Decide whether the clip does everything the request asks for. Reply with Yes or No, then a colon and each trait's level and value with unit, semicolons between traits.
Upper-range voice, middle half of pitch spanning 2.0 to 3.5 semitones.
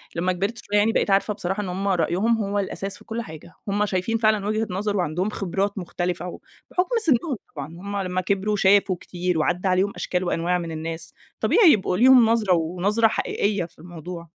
Yes: high, 195 Hz; average, 3.0 semitones